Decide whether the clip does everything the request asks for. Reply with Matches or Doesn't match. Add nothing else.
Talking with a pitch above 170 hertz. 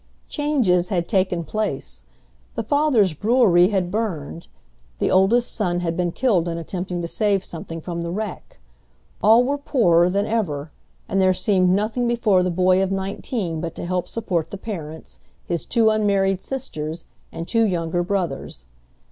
Matches